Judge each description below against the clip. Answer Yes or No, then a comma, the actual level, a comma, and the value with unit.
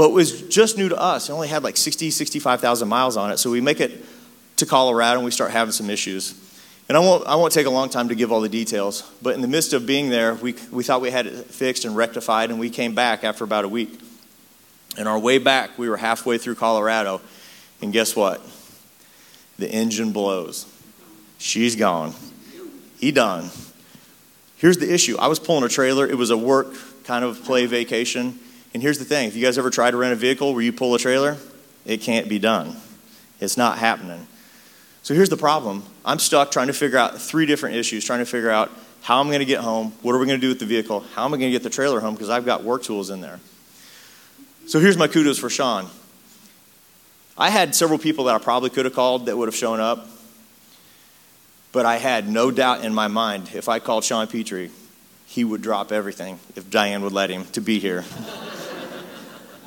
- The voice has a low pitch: Yes, low, 120 Hz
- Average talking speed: No, fast, 220 wpm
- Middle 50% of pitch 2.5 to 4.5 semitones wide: Yes, average, 3.6 semitones